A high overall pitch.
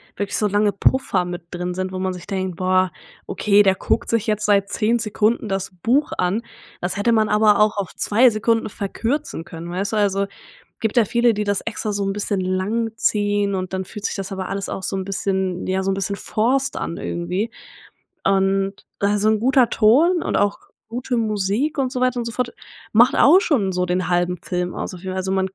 Yes: high, 205 Hz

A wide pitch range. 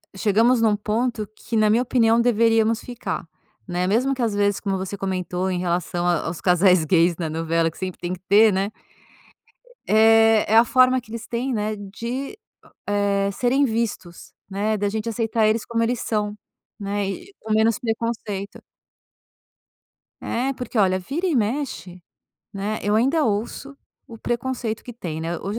No: average, 3.3 semitones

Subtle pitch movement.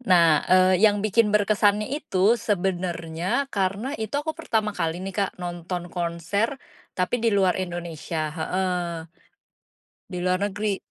No: average, 3.2 semitones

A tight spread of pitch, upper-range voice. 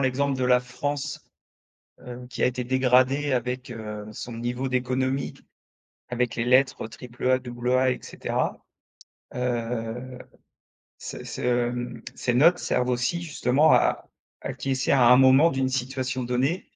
No: narrow, 1.3 semitones; low, 125 Hz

